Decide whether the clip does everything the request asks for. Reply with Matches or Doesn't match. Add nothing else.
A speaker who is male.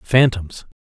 Matches